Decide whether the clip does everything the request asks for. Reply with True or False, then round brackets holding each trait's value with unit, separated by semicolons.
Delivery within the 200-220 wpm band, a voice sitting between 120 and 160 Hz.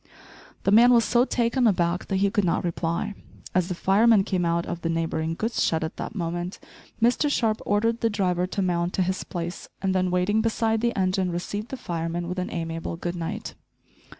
False (205 wpm; 185 Hz)